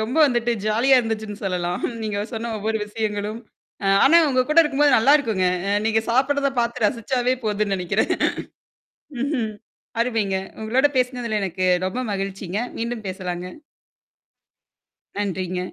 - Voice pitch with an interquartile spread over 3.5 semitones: Yes, average, 3.9 semitones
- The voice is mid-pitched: No, high, 220 Hz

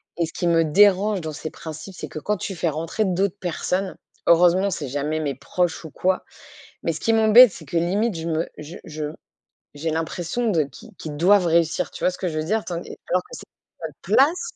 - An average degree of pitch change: Yes, average, 3.8 semitones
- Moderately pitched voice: Yes, medium, 175 Hz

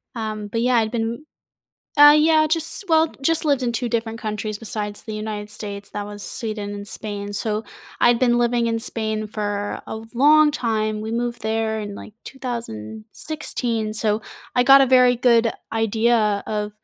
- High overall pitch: Yes, high, 225 Hz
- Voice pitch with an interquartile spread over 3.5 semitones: No, average, 2.7 semitones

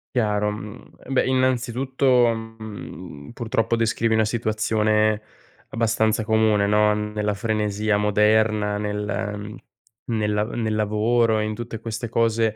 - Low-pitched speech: Yes, low, 110 Hz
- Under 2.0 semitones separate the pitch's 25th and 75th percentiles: Yes, narrow, 1.5 semitones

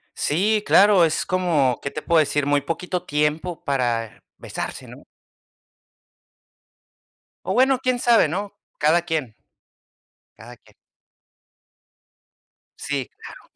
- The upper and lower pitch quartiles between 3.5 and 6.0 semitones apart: Yes, average, 4.7 semitones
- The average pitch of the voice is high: No, medium, 160 Hz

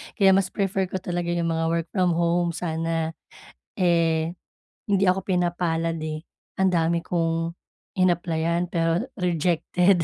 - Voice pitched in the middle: Yes, medium, 170 Hz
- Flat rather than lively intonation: Yes, narrow, 1.5 semitones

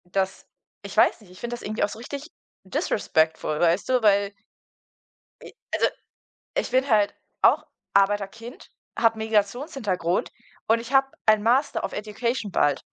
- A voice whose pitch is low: No, high, 215 Hz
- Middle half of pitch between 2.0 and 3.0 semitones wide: No, average, 3.5 semitones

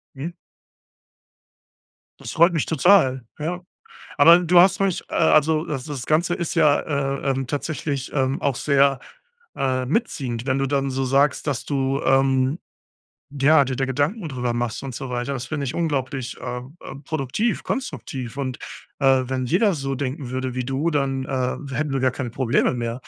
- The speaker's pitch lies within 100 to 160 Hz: Yes, low, 135 Hz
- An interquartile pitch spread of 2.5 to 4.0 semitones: Yes, average, 2.8 semitones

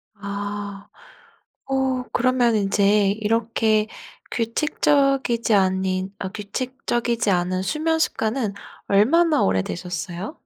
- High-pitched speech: Yes, high, 215 Hz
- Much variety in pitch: No, average, 4.4 semitones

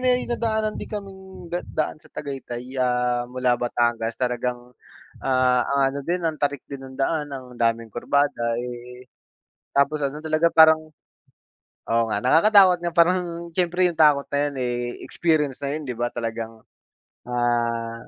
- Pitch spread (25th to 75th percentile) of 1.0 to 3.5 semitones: No, average, 5.0 semitones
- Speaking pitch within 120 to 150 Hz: Yes, low, 135 Hz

